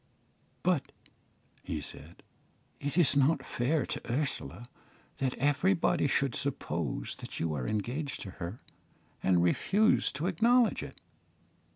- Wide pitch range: Yes, wide, 8.1 semitones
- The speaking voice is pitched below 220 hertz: Yes, medium, 140 Hz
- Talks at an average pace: No, slow, 125 wpm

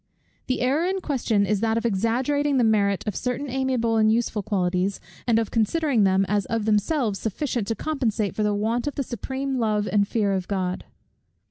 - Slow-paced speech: No, average, 195 wpm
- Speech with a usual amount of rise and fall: Yes, average, 4.0 semitones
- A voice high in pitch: Yes, high, 225 Hz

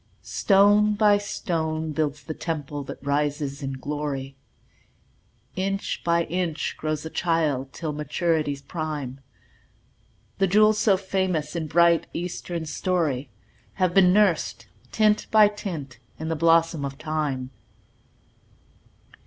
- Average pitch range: Yes, average, 4.1 semitones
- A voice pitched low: No, medium, 160 Hz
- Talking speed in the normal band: No, slow, 120 wpm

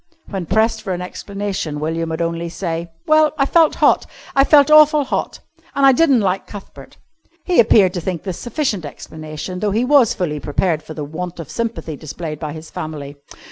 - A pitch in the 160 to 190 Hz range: Yes, medium, 185 Hz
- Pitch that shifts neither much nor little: No, wide, 6.8 semitones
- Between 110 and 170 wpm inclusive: No, average, 190 wpm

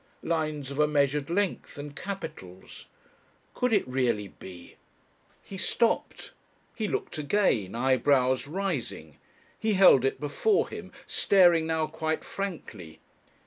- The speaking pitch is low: No, medium, 150 Hz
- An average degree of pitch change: No, wide, 6.3 semitones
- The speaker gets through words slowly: Yes, slow, 120 wpm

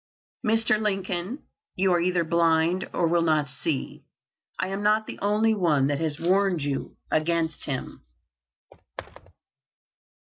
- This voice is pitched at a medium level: Yes, medium, 175 Hz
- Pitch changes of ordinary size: Yes, average, 3.6 semitones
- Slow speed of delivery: Yes, slow, 125 wpm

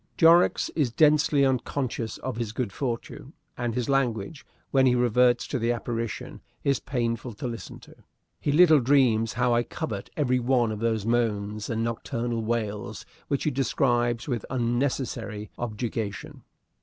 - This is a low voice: Yes, low, 120 Hz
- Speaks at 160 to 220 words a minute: No, average, 150 wpm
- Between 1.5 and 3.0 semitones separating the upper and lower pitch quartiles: Yes, narrow, 2.6 semitones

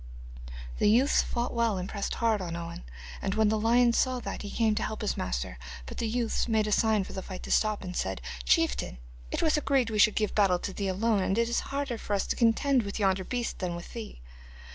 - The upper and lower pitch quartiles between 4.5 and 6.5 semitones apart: No, average, 3.5 semitones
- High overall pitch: Yes, high, 215 Hz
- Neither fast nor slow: No, fast, 240 wpm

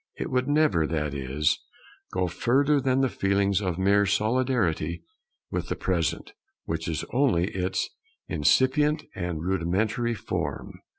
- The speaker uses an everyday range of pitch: No, wide, 7.1 semitones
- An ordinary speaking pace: No, slow, 130 wpm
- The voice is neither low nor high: No, low, 100 Hz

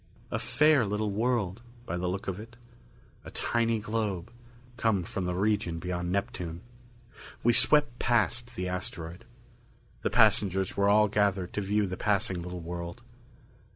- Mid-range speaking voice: No, low, 100 Hz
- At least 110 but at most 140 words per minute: No, average, 150 wpm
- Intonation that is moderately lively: Yes, average, 4.1 semitones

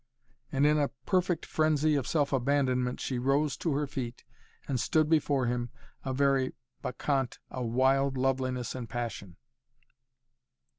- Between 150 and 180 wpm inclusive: No, average, 140 wpm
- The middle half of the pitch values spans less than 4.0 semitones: Yes, narrow, 2.5 semitones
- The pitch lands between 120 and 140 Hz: Yes, low, 135 Hz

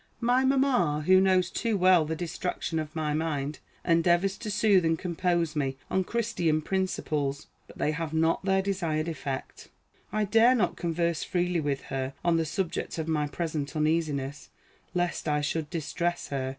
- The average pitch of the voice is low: No, medium, 165 Hz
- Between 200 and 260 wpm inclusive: No, average, 165 wpm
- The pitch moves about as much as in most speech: Yes, average, 3.5 semitones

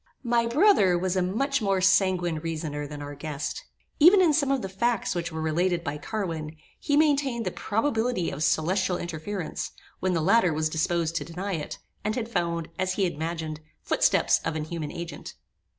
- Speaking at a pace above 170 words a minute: Yes, average, 180 wpm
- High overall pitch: No, medium, 180 Hz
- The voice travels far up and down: Yes, wide, 5.7 semitones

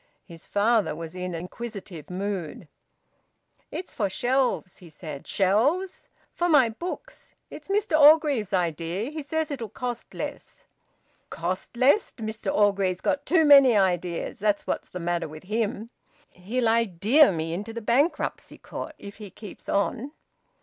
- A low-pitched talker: No, high, 210 Hz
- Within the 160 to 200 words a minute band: No, average, 145 wpm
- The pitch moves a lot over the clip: Yes, wide, 6.7 semitones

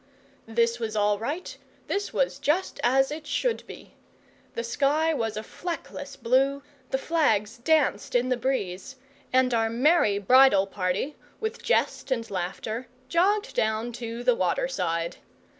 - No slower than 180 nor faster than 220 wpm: No, average, 145 wpm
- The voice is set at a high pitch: Yes, high, 245 Hz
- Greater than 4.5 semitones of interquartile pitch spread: Yes, average, 4.9 semitones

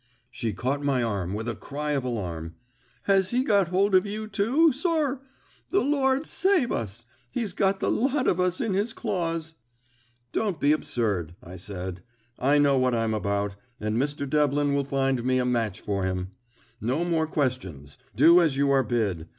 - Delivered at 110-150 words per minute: No, average, 180 wpm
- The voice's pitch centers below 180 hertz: Yes, medium, 140 Hz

